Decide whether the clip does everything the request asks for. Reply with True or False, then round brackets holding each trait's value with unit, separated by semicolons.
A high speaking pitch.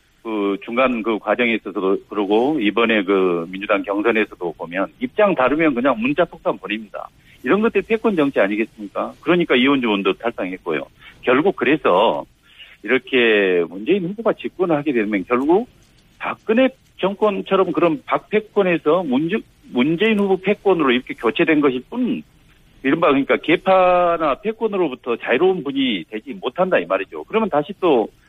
False (150 Hz)